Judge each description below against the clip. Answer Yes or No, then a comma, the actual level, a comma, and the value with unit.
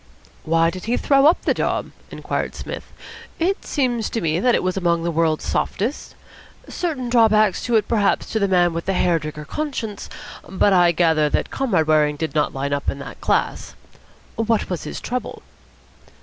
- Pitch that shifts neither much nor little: No, wide, 6.1 semitones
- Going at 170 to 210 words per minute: Yes, average, 185 wpm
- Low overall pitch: No, medium, 185 Hz